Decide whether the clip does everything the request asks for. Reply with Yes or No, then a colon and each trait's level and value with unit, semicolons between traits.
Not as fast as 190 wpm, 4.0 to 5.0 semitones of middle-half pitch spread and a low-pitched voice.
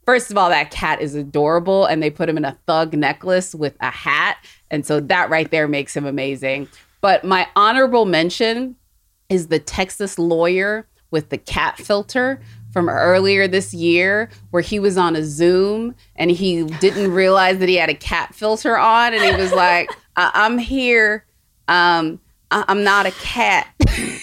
No: average, 180 wpm; average, 4.3 semitones; medium, 180 Hz